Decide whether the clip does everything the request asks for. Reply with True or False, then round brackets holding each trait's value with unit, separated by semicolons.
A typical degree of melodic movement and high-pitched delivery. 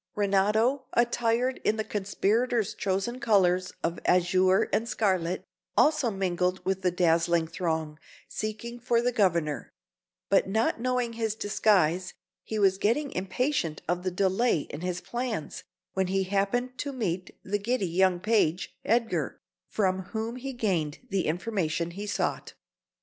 True (4.3 semitones; 195 Hz)